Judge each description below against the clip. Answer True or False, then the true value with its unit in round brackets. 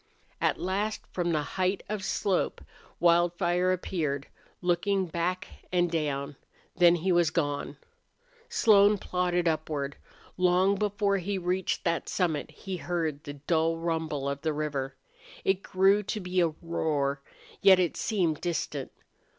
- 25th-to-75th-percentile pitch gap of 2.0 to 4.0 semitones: True (3.1 semitones)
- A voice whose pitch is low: False (175 Hz)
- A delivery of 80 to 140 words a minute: True (135 wpm)